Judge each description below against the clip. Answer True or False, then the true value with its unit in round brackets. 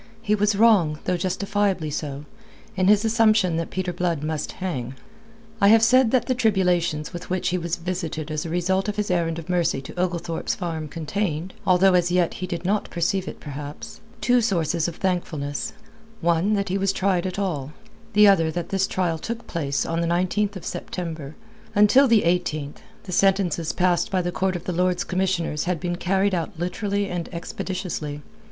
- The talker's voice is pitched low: False (180 Hz)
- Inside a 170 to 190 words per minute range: True (185 wpm)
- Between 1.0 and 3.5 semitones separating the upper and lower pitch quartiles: True (3.0 semitones)